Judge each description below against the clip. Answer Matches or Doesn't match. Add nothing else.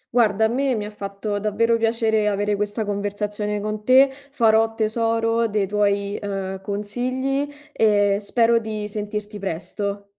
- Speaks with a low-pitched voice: Doesn't match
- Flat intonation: Matches